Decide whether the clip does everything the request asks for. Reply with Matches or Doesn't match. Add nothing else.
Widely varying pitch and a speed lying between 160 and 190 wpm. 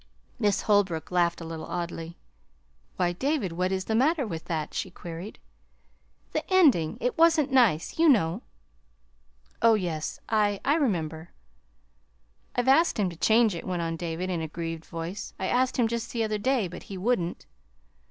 Matches